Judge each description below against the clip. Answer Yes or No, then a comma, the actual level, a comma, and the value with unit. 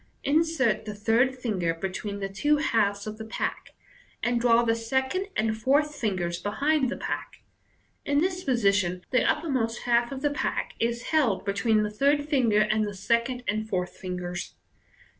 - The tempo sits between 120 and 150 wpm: No, average, 175 wpm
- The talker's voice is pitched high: Yes, high, 230 Hz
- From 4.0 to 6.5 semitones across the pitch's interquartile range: Yes, average, 4.6 semitones